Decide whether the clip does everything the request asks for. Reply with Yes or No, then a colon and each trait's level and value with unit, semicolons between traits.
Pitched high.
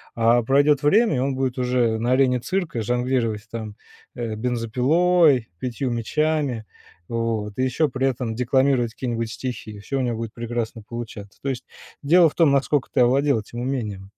No: low, 125 Hz